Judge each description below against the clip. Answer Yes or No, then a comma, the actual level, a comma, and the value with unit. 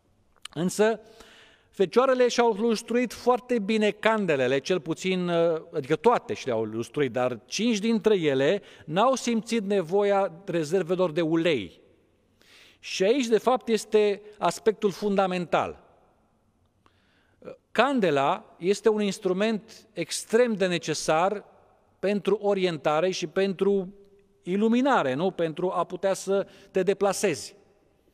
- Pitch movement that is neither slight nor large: Yes, average, 3.9 semitones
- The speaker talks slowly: Yes, slow, 105 wpm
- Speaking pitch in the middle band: No, high, 195 Hz